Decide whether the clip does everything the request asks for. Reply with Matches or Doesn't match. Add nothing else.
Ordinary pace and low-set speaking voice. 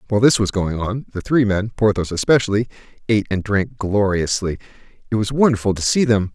Matches